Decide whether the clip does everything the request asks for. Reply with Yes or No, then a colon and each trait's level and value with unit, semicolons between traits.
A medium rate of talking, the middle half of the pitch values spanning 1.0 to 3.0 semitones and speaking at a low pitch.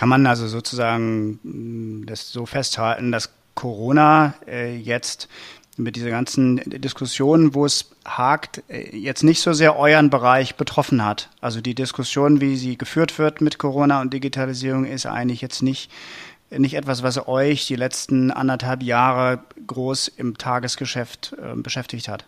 Yes: average, 145 wpm; narrow, 2.5 semitones; low, 130 Hz